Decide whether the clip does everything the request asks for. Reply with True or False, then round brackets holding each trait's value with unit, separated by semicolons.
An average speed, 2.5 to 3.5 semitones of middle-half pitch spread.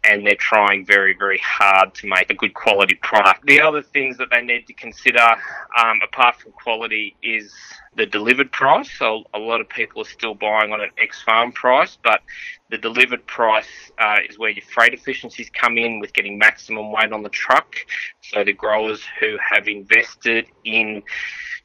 True (185 wpm; 3.0 semitones)